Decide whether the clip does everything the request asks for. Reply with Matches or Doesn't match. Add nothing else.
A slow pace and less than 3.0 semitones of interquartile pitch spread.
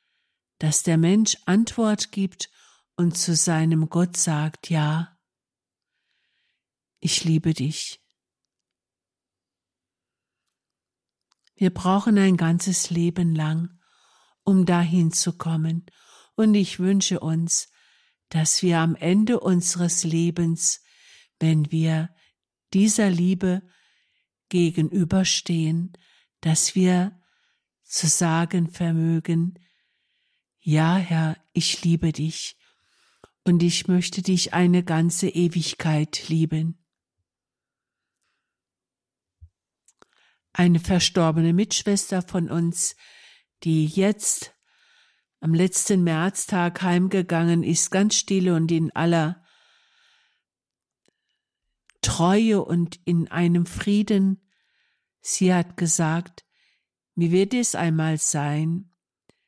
Matches